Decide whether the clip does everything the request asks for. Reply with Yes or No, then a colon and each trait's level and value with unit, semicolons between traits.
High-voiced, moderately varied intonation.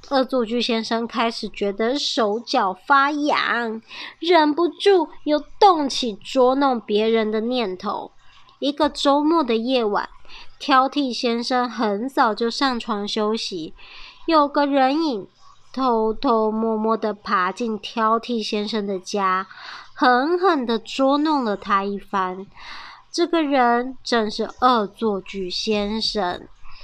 Yes: high, 240 Hz; average, 4.4 semitones